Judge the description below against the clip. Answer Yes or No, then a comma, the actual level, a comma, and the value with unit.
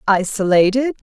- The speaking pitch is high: Yes, high, 210 Hz